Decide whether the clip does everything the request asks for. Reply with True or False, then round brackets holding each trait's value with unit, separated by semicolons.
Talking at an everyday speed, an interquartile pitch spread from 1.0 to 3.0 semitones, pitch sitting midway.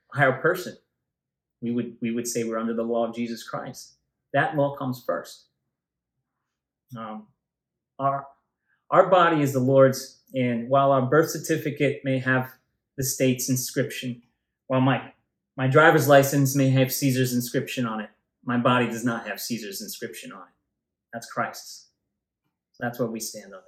False (160 wpm; 2.6 semitones; 130 Hz)